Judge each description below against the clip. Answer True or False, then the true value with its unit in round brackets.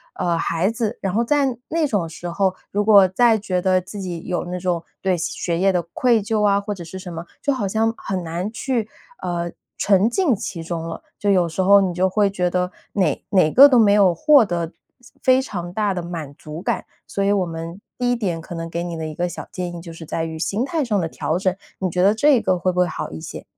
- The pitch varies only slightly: False (3.5 semitones)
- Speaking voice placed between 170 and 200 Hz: True (185 Hz)